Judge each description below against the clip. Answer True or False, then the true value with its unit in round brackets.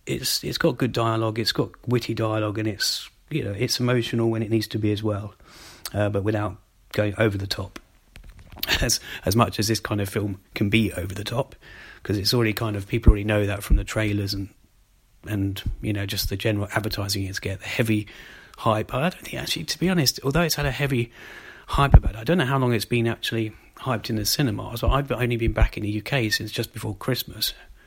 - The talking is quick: True (230 wpm)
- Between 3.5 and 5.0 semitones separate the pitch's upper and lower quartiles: False (2.5 semitones)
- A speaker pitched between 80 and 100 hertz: False (110 Hz)